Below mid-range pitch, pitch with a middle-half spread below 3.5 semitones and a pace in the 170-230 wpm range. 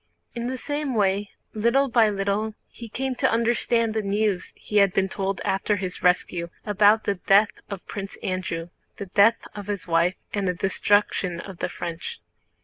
No: high, 205 Hz; average, 2.8 semitones; average, 175 wpm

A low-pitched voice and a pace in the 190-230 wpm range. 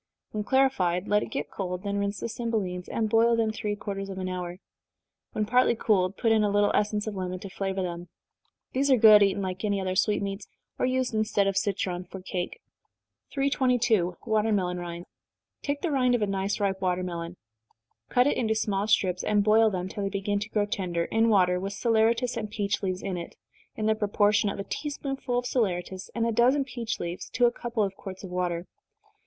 No: high, 205 Hz; fast, 205 wpm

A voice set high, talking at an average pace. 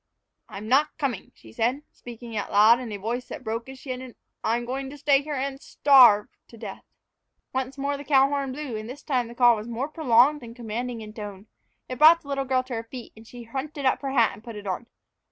No: very high, 250 Hz; fast, 240 wpm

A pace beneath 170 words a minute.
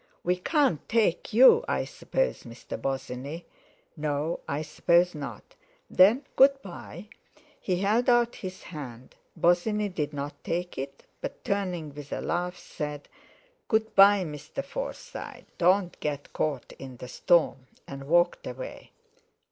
Yes: slow, 135 wpm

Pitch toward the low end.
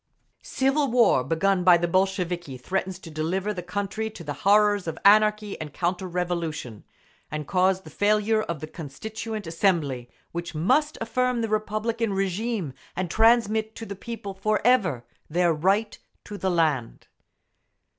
No: high, 190 Hz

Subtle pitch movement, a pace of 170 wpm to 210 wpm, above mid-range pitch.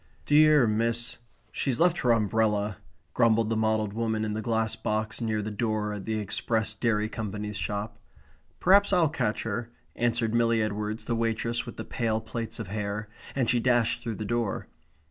No: narrow, 1.7 semitones; average, 175 wpm; low, 110 Hz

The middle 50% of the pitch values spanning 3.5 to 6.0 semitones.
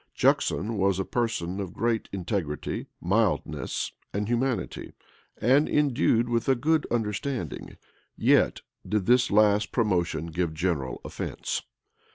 Yes: average, 4.7 semitones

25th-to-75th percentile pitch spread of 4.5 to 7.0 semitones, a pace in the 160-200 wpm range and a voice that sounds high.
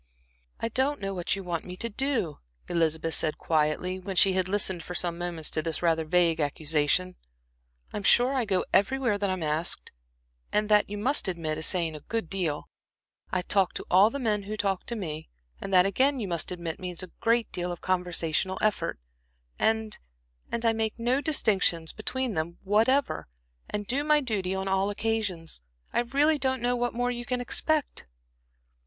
Yes: average, 5.1 semitones; average, 185 wpm; high, 195 Hz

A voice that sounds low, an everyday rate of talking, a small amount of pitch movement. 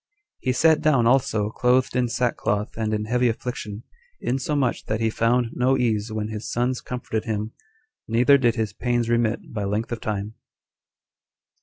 Yes: low, 115 Hz; average, 160 wpm; narrow, 2.3 semitones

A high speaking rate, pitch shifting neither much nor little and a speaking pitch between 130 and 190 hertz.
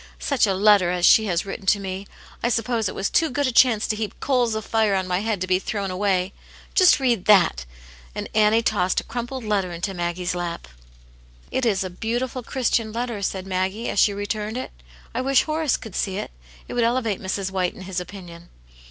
No: fast, 220 wpm; average, 3.8 semitones; high, 205 Hz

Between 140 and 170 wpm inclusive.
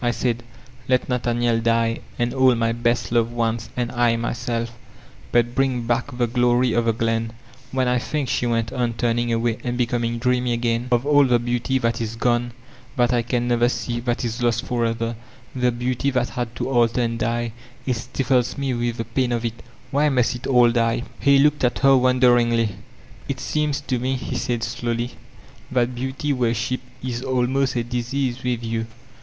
No: average, 195 wpm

